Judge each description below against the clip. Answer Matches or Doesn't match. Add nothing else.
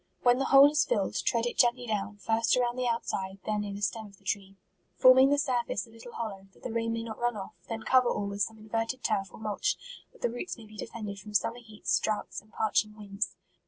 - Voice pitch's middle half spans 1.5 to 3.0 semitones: Matches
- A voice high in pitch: Matches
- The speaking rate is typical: Doesn't match